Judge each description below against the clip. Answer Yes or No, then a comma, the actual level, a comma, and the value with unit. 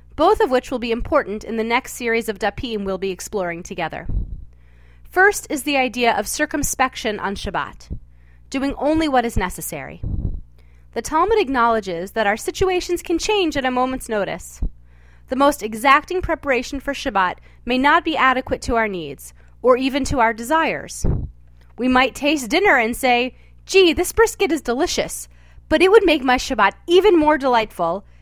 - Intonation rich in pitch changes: Yes, wide, 8.1 semitones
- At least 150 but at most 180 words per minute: Yes, average, 170 wpm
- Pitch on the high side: Yes, high, 245 Hz